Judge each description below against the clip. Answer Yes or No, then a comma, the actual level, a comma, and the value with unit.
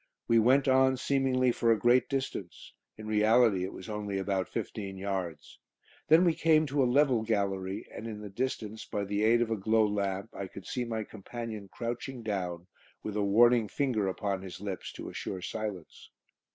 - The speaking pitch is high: No, low, 110 Hz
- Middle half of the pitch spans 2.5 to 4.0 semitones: Yes, average, 3.7 semitones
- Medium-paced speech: Yes, average, 185 wpm